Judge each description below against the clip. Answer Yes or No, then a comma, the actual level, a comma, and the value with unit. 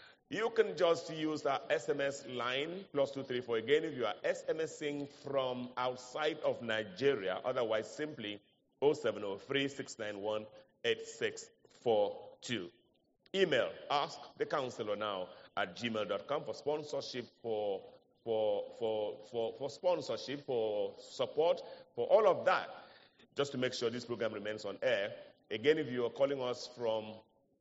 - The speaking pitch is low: No, medium, 150 Hz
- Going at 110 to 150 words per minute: Yes, slow, 135 wpm